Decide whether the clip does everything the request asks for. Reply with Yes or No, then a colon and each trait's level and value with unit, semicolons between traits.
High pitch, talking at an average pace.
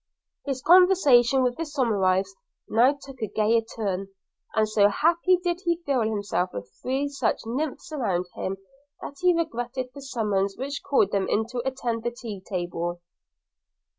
Yes: high, 240 Hz; average, 165 wpm